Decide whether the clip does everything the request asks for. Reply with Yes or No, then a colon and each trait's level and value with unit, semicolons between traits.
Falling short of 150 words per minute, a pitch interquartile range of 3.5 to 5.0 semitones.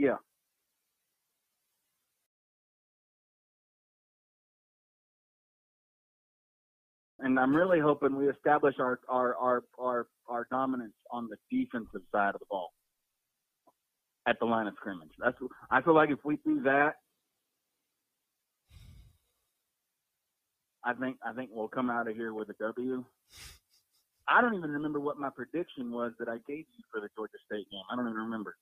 Yes: average, 140 wpm; average, 3.8 semitones